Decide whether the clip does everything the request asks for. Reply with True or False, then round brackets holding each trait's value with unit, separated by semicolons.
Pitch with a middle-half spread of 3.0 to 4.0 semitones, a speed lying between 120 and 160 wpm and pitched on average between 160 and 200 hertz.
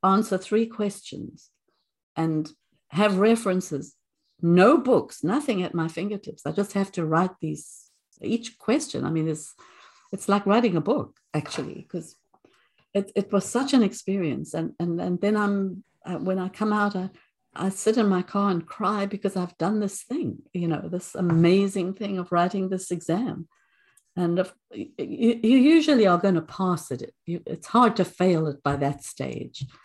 False (3.3 semitones; 170 wpm; 190 Hz)